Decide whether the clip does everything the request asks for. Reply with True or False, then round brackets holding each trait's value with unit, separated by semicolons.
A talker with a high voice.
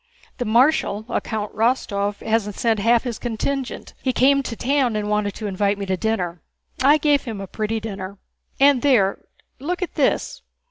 True (225 Hz)